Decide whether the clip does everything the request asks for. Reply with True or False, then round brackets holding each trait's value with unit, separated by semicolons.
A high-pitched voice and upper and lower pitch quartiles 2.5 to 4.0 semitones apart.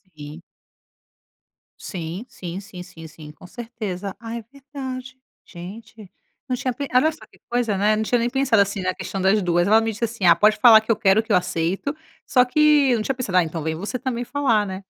False (215 Hz; 5.1 semitones)